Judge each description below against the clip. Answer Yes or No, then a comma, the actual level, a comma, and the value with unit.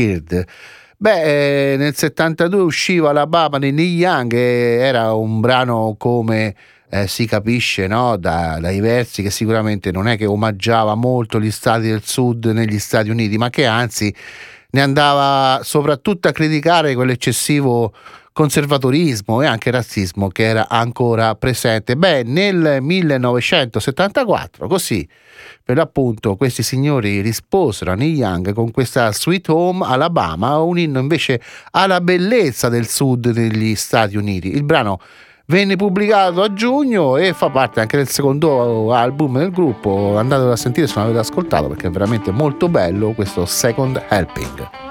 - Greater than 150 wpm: No, average, 145 wpm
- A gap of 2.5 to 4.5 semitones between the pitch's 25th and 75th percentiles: No, average, 5.3 semitones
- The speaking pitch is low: Yes, low, 125 Hz